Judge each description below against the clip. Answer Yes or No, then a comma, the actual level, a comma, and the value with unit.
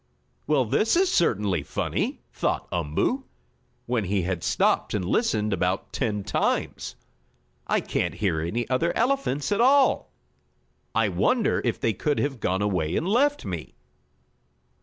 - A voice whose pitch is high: No, low, 115 Hz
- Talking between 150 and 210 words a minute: No, average, 140 wpm